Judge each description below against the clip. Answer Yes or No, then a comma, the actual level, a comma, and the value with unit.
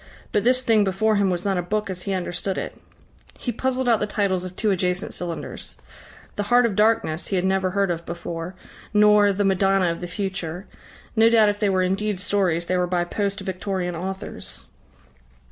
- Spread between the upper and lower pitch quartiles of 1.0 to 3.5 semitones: Yes, narrow, 2.6 semitones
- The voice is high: Yes, high, 195 Hz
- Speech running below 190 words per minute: No, average, 195 wpm